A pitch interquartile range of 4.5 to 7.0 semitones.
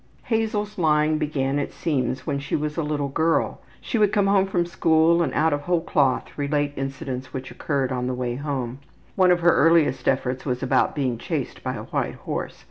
No: average, 4.1 semitones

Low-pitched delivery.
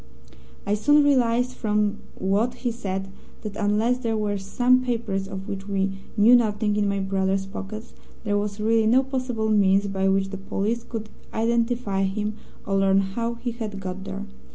No: high, 210 Hz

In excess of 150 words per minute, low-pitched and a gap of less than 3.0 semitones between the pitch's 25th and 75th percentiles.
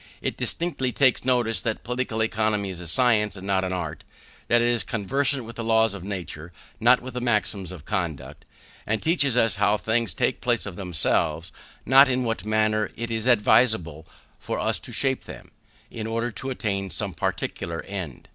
No: average, 180 wpm; low, 110 Hz; average, 4.1 semitones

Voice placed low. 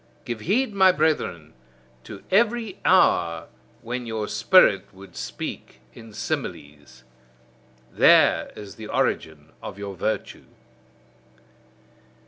Yes: low, 110 Hz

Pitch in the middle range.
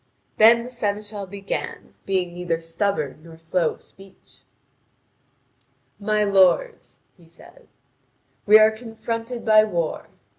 No: high, 200 Hz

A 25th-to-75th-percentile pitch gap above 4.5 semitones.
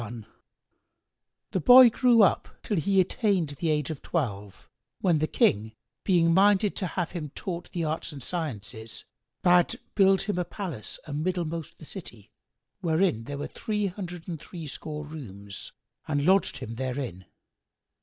Yes: average, 4.9 semitones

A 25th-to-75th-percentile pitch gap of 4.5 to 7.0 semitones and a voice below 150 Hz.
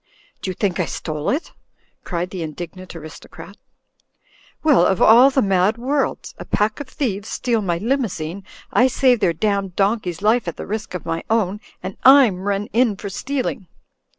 No: average, 5.0 semitones; high, 200 Hz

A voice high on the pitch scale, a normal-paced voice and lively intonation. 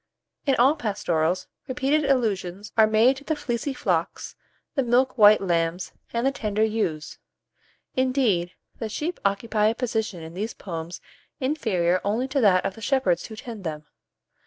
Yes: high, 220 Hz; average, 160 wpm; wide, 5.9 semitones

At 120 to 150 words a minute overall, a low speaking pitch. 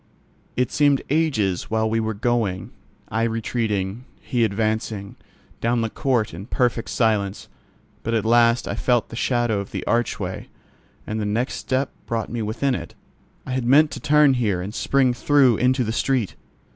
No: average, 170 wpm; low, 115 Hz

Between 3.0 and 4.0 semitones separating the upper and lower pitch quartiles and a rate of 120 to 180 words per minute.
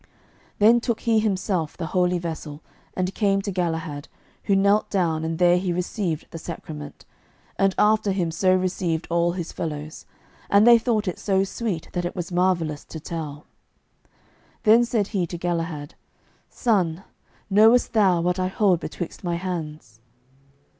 Yes: average, 3.4 semitones; average, 155 wpm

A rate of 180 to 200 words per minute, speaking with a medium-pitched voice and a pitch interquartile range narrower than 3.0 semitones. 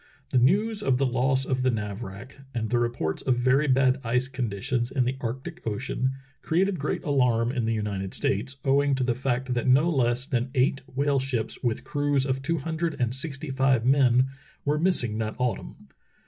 No: average, 190 wpm; low, 130 Hz; narrow, 2.5 semitones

